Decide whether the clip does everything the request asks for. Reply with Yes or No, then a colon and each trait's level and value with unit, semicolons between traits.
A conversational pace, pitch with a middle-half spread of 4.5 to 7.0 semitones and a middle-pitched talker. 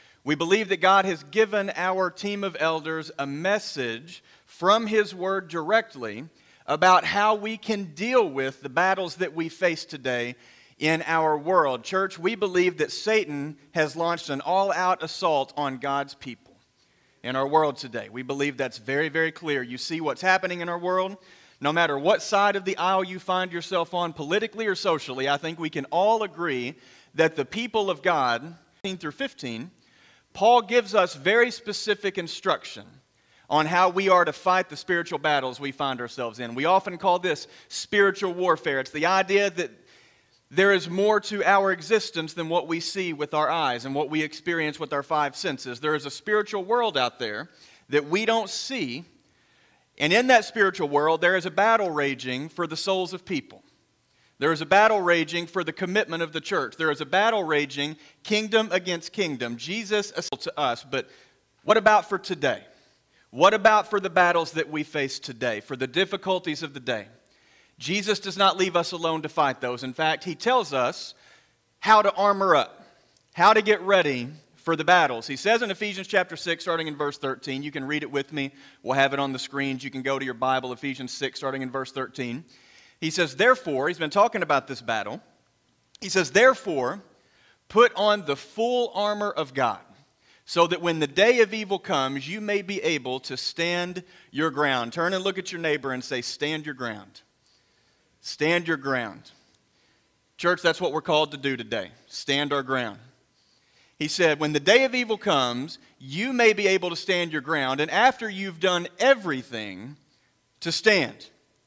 Yes: average, 190 wpm; wide, 5.6 semitones; medium, 165 Hz